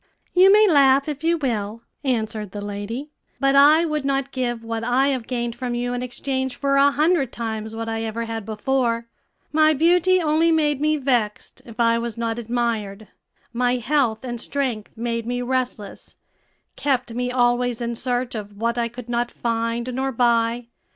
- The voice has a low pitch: No, high, 245 Hz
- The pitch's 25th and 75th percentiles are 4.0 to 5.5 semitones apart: No, average, 3.1 semitones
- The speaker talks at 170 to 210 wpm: Yes, average, 180 wpm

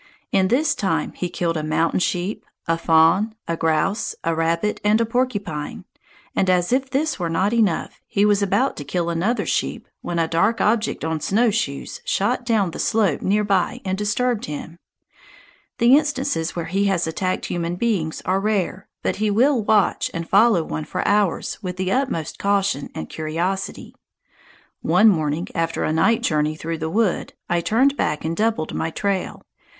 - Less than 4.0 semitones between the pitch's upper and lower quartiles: No, average, 4.8 semitones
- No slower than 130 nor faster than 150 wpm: No, average, 175 wpm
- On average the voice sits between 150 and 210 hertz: Yes, high, 190 Hz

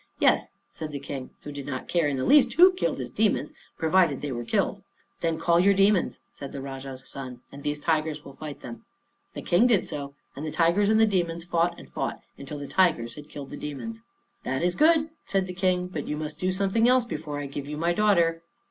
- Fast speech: Yes, fast, 230 wpm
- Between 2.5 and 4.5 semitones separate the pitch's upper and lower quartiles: No, average, 4.9 semitones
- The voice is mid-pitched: Yes, medium, 160 Hz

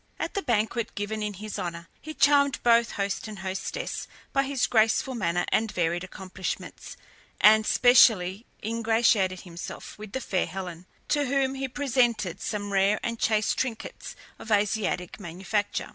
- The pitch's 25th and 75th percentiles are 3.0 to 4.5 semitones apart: Yes, average, 4.0 semitones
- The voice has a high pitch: Yes, high, 215 Hz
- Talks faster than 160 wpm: No, average, 150 wpm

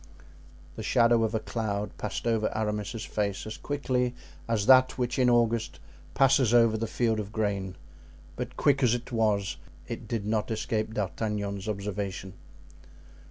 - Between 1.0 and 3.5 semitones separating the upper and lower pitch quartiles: Yes, narrow, 2.4 semitones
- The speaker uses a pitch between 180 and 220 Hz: No, low, 110 Hz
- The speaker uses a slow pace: No, average, 150 wpm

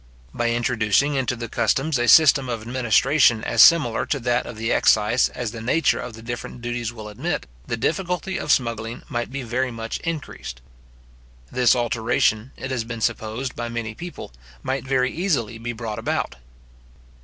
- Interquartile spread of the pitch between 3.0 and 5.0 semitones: No, narrow, 2.6 semitones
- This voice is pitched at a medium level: No, low, 120 Hz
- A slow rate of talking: No, average, 170 wpm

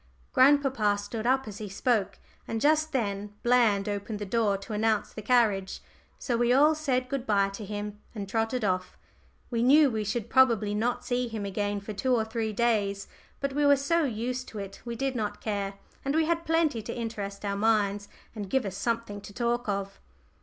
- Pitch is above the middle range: Yes, high, 225 Hz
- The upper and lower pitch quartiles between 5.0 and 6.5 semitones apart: No, average, 3.7 semitones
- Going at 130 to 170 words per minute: No, fast, 205 wpm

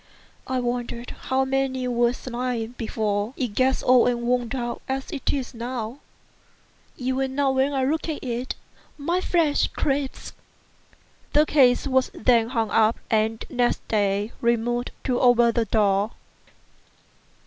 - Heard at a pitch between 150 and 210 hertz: No, high, 245 Hz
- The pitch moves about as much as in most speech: No, narrow, 2.3 semitones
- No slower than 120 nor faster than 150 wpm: Yes, average, 140 wpm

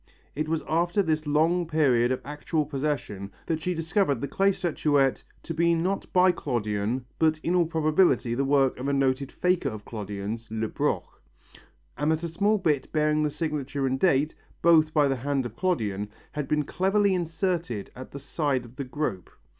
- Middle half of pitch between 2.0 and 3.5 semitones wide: No, average, 4.2 semitones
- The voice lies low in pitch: No, medium, 150 Hz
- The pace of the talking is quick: No, average, 180 wpm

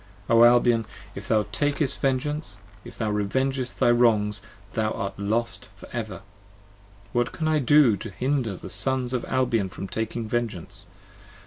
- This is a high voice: No, low, 120 Hz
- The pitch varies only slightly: No, average, 3.7 semitones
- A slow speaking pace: No, average, 150 wpm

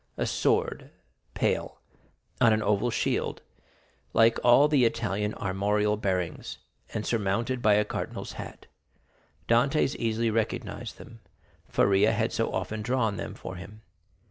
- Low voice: Yes, low, 110 Hz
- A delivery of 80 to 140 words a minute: Yes, slow, 135 wpm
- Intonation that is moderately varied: No, narrow, 2.2 semitones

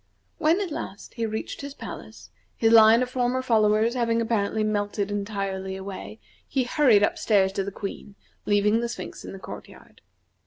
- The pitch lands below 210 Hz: No, high, 215 Hz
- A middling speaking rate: Yes, average, 180 wpm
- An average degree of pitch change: Yes, average, 3.0 semitones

